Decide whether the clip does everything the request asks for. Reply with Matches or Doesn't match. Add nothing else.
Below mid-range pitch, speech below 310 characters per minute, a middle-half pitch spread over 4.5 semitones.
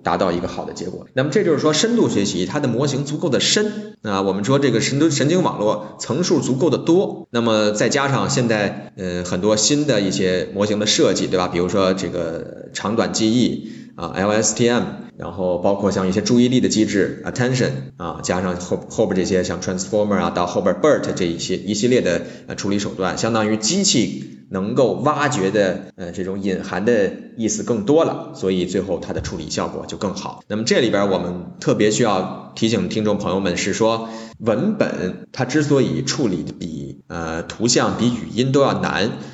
Doesn't match